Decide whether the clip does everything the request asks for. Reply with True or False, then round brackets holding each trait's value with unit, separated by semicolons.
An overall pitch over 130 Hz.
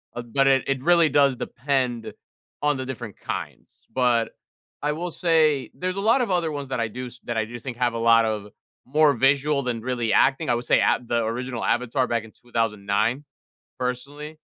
False (125 Hz)